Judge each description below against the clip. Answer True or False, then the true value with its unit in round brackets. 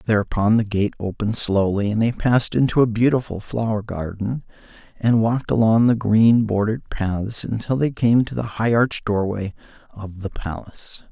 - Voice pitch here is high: False (110 Hz)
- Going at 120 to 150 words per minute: False (165 wpm)